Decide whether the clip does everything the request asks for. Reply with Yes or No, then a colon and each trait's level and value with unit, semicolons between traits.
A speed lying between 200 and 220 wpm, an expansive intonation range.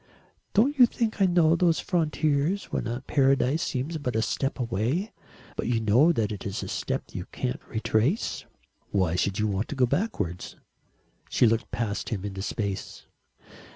No: average, 165 wpm; wide, 7.5 semitones